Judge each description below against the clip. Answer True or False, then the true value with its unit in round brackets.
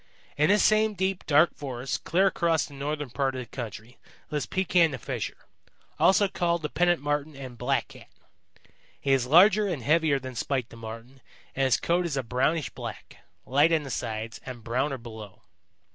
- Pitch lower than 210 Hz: True (140 Hz)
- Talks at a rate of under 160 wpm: False (180 wpm)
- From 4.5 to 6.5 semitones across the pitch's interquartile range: True (5.0 semitones)